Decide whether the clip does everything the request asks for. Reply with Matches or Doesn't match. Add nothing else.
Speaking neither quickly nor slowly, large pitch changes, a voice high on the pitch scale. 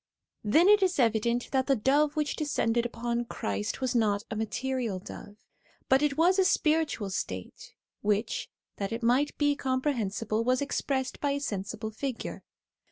Doesn't match